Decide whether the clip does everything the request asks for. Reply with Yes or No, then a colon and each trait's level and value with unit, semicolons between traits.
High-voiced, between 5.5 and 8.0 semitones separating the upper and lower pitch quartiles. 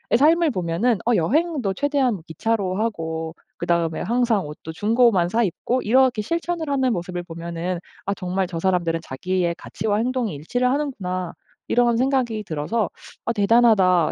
Yes: high, 205 Hz; wide, 6.0 semitones